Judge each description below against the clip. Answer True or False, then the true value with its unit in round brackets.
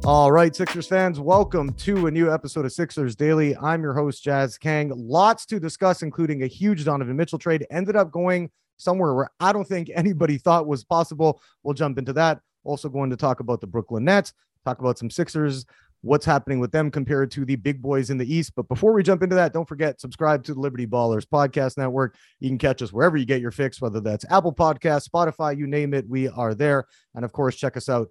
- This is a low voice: False (145 Hz)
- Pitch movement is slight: False (3.9 semitones)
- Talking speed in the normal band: False (230 wpm)